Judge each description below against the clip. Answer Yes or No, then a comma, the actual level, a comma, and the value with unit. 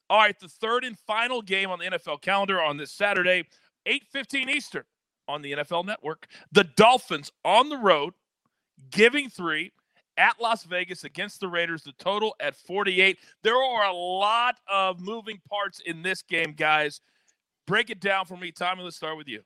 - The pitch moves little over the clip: No, average, 4.4 semitones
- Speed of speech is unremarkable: Yes, average, 180 wpm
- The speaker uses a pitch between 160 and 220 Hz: Yes, high, 190 Hz